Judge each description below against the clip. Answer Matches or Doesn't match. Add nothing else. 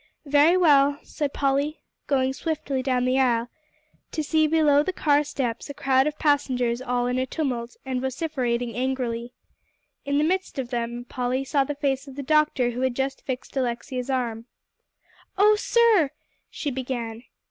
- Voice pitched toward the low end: Doesn't match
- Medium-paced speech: Matches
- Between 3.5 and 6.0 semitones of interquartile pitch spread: Doesn't match